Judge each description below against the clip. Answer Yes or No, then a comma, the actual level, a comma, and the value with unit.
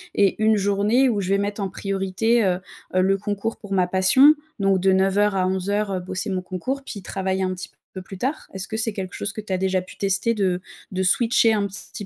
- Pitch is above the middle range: Yes, high, 195 Hz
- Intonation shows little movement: Yes, narrow, 2.1 semitones